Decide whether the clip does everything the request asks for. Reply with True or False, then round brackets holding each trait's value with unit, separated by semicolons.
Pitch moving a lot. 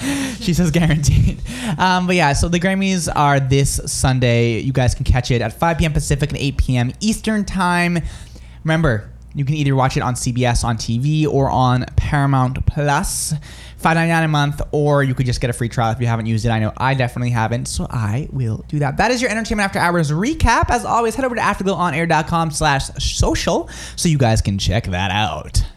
True (5.9 semitones)